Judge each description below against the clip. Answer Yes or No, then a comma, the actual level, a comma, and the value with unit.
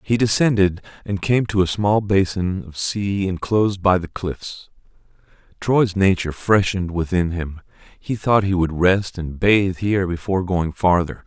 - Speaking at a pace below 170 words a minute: Yes, average, 160 wpm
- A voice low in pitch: Yes, very low, 95 Hz